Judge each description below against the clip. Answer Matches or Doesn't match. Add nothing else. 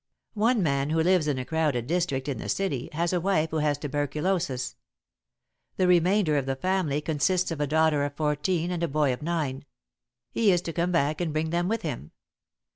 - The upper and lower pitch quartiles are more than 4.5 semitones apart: Doesn't match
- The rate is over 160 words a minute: Matches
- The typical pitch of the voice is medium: Matches